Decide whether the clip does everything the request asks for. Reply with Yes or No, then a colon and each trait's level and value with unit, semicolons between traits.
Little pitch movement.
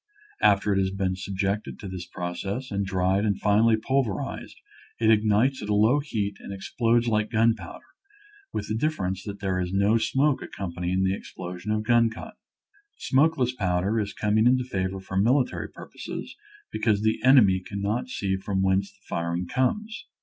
No: average, 3.4 semitones